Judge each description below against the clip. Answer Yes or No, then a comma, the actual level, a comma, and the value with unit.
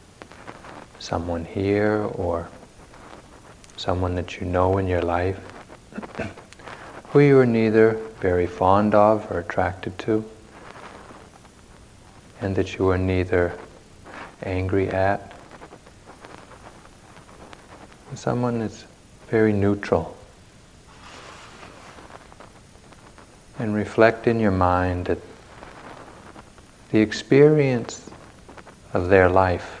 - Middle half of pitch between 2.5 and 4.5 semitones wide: Yes, average, 3.4 semitones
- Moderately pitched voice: No, low, 100 Hz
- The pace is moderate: No, slow, 85 wpm